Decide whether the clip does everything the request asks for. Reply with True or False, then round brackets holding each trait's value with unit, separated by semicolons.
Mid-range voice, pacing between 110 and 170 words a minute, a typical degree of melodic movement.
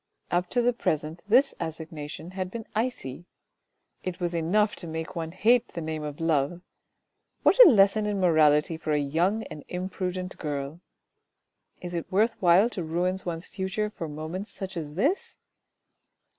True (175 Hz; 160 wpm; 4.1 semitones)